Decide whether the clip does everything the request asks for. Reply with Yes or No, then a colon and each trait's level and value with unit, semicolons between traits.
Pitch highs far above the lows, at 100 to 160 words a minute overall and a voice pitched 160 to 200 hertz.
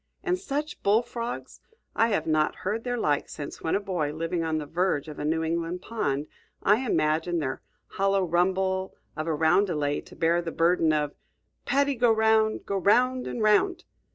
No: wide, 5.7 semitones; average, 180 wpm; medium, 185 Hz